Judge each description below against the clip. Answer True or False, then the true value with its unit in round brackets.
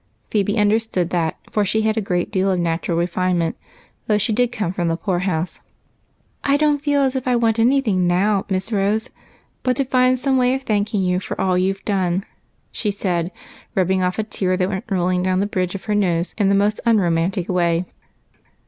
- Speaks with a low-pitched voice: False (195 Hz)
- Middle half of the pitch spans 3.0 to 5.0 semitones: True (3.5 semitones)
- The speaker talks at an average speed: False (210 wpm)